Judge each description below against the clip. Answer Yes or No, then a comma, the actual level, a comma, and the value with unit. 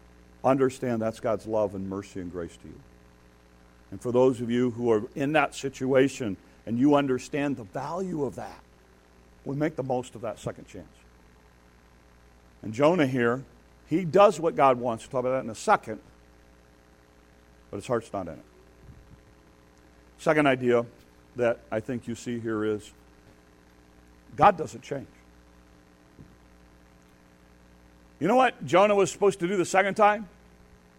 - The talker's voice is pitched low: Yes, very low, 85 Hz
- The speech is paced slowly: No, average, 155 wpm